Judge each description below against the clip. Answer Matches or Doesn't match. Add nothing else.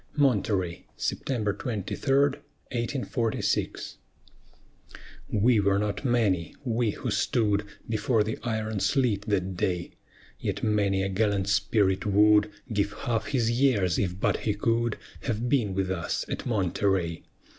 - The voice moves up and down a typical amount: Matches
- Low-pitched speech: Matches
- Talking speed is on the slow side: Matches